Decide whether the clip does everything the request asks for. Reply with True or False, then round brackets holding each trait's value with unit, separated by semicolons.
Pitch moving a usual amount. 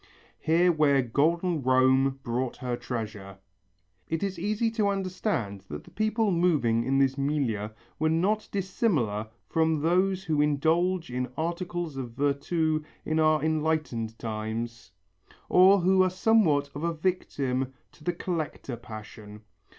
False (6.0 semitones)